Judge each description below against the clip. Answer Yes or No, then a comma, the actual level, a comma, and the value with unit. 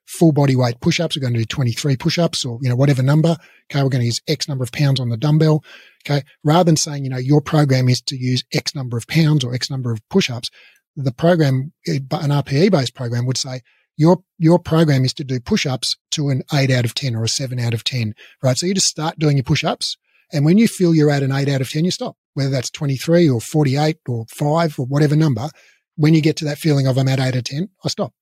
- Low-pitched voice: No, medium, 145 Hz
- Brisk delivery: Yes, fast, 255 wpm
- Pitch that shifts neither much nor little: Yes, average, 3.7 semitones